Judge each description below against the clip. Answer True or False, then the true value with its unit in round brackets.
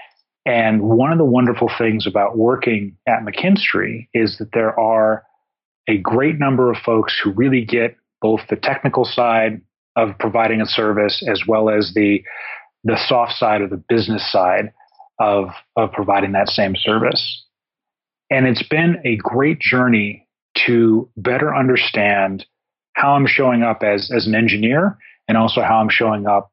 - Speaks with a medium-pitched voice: False (115 Hz)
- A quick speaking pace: False (160 wpm)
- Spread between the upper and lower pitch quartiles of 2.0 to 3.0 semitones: True (2.7 semitones)